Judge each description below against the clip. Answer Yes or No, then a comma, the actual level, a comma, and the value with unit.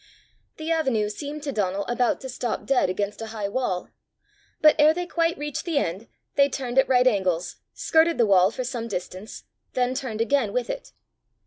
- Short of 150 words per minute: No, average, 190 wpm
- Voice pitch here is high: Yes, high, 245 Hz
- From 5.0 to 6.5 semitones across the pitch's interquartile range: Yes, wide, 5.4 semitones